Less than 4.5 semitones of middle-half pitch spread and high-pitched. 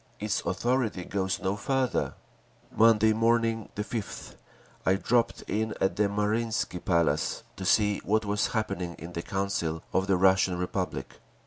No: average, 2.9 semitones; low, 100 Hz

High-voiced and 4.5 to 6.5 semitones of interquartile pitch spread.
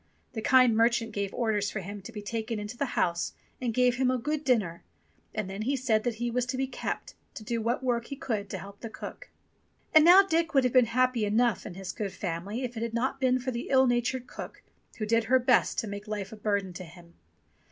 No: high, 230 Hz; average, 3.5 semitones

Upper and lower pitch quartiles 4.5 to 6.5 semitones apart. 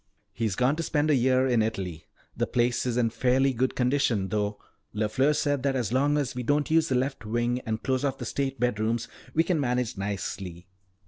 No: average, 3.7 semitones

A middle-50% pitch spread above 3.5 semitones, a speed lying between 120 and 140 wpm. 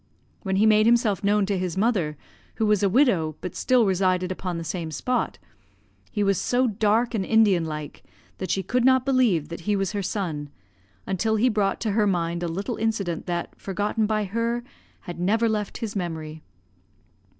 No: average, 3.9 semitones; average, 185 wpm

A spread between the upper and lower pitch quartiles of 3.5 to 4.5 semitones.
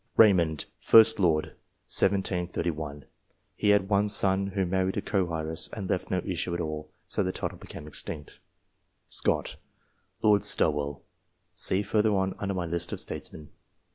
Yes: average, 3.8 semitones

